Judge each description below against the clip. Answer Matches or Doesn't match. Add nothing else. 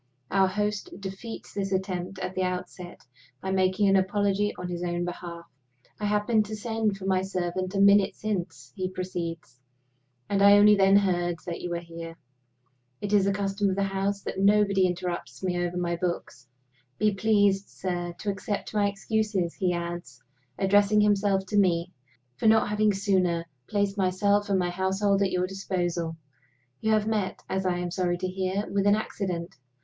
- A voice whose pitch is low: Doesn't match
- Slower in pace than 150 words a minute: Doesn't match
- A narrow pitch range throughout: Matches